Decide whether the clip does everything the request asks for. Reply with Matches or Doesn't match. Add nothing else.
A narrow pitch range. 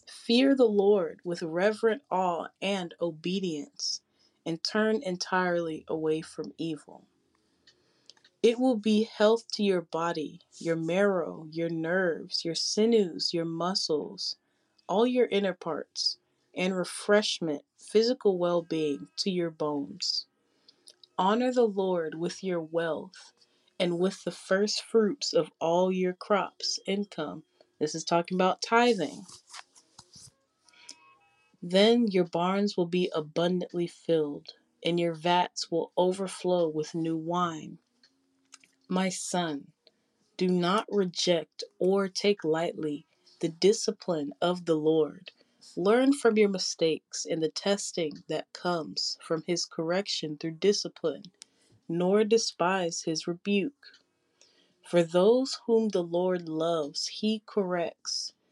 Doesn't match